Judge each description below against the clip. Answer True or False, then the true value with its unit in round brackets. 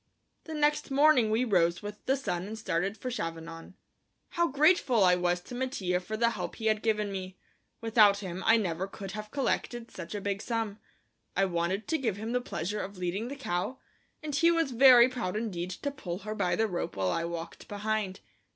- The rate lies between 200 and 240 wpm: True (205 wpm)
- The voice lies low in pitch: False (210 Hz)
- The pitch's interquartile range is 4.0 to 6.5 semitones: True (5.2 semitones)